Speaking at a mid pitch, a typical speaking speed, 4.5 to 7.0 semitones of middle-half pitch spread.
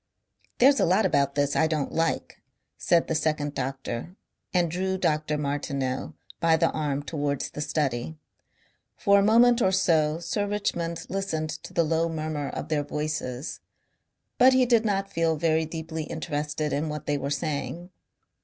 No: medium, 155 Hz; average, 165 wpm; average, 3.0 semitones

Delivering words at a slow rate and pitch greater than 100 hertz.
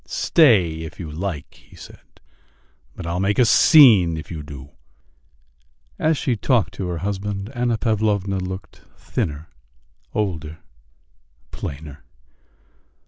No: slow, 125 wpm; very low, 95 Hz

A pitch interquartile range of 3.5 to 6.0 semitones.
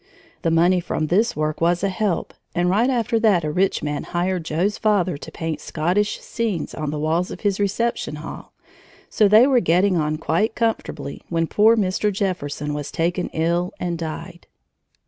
Yes: average, 4.3 semitones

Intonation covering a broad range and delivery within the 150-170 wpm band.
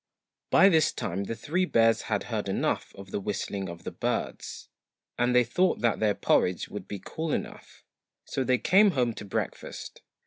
No: wide, 7.5 semitones; average, 180 wpm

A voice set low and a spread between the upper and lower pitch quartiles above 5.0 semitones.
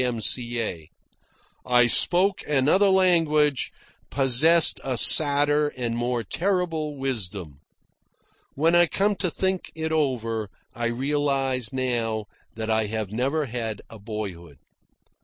Yes: low, 130 Hz; wide, 5.4 semitones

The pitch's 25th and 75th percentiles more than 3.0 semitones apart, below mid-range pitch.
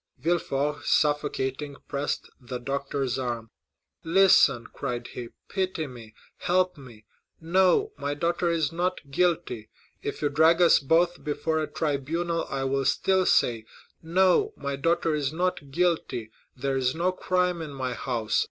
No: average, 4.5 semitones; medium, 150 Hz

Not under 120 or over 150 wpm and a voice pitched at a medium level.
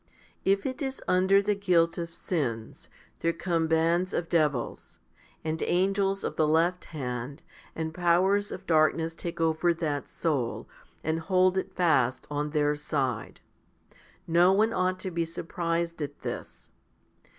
Yes: average, 145 wpm; medium, 165 Hz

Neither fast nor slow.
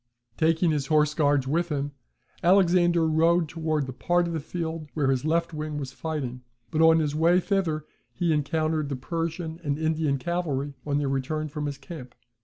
Yes: average, 185 wpm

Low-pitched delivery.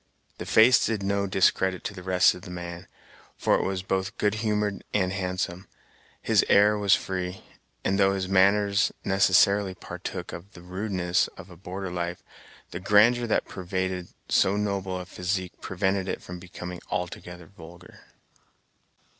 Yes: very low, 95 Hz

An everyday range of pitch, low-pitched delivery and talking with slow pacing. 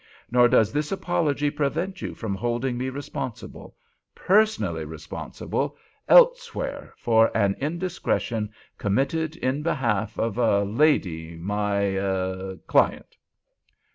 No: wide, 7.0 semitones; low, 120 Hz; slow, 85 wpm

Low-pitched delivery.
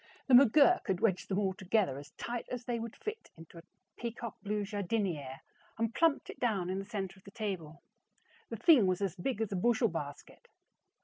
No: high, 205 Hz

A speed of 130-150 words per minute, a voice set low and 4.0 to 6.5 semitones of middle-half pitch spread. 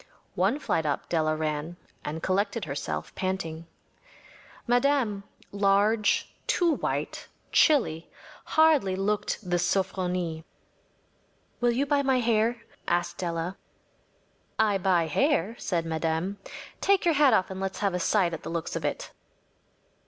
No: slow, 135 wpm; high, 190 Hz; wide, 5.6 semitones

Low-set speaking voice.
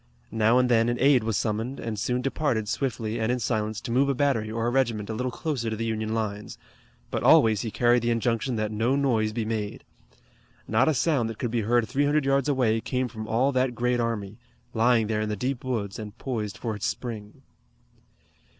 Yes: low, 115 Hz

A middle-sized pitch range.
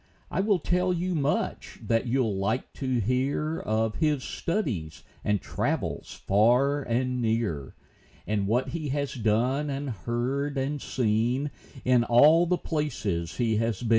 Yes: average, 4.7 semitones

